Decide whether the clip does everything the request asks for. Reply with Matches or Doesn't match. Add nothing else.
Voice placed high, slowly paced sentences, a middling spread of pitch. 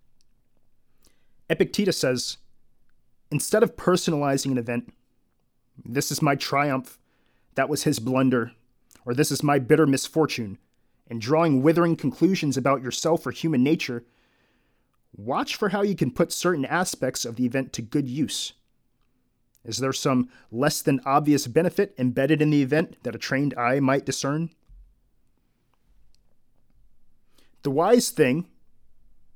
Doesn't match